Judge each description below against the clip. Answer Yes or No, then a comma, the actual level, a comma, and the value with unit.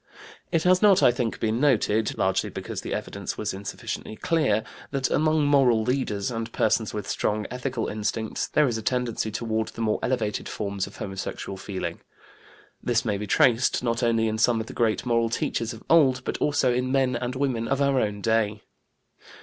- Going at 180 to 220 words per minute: Yes, average, 190 wpm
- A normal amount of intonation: Yes, average, 3.1 semitones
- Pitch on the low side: Yes, low, 115 Hz